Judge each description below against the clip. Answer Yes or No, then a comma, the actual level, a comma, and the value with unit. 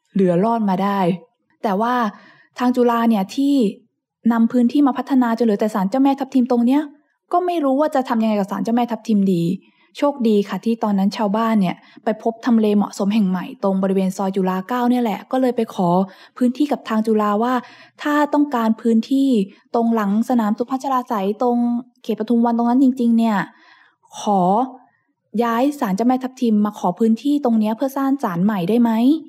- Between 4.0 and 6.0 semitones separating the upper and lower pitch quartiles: No, average, 3.3 semitones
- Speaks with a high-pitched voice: Yes, high, 230 Hz